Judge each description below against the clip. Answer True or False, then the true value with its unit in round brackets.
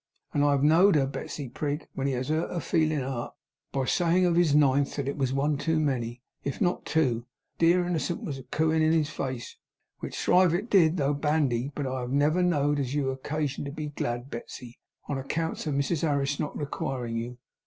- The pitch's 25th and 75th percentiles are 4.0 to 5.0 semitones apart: False (3.0 semitones)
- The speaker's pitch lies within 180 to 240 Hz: False (145 Hz)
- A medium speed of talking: False (215 wpm)